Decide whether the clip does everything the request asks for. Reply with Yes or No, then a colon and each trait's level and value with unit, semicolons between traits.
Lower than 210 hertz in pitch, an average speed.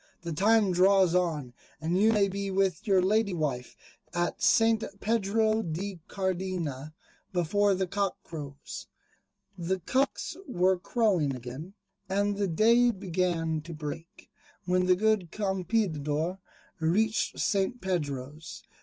No: medium, 185 Hz; slow, 125 wpm